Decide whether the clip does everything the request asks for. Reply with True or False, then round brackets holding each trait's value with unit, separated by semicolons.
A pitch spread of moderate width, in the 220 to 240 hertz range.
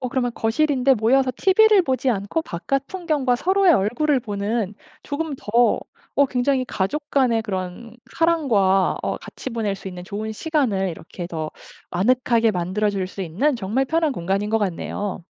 False (6.0 semitones; 235 Hz)